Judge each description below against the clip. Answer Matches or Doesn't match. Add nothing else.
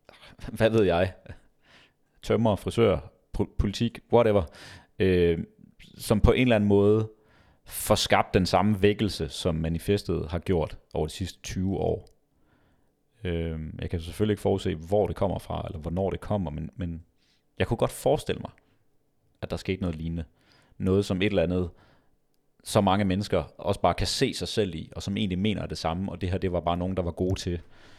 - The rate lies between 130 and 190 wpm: Matches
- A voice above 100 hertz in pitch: Doesn't match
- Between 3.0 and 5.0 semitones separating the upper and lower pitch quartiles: Matches